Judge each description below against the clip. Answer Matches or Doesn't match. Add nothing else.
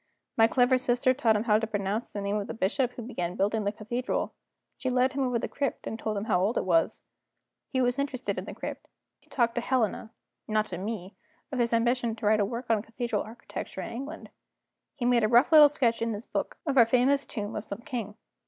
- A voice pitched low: Doesn't match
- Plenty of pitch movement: Doesn't match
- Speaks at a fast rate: Matches